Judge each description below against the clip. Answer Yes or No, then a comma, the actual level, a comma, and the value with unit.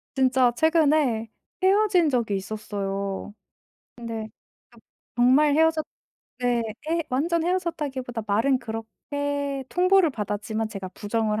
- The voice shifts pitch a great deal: Yes, wide, 6.0 semitones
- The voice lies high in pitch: Yes, very high, 255 Hz